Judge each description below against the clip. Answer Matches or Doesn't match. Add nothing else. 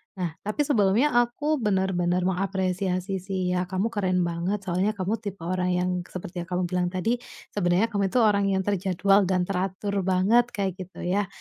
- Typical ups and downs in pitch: Doesn't match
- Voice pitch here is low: Doesn't match